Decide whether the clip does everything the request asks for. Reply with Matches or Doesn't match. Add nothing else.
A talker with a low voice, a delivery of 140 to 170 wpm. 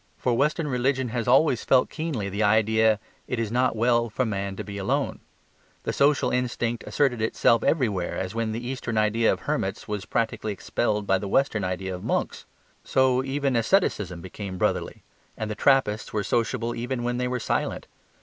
Doesn't match